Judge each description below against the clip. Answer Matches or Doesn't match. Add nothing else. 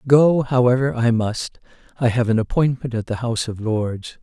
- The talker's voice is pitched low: Matches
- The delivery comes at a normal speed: Matches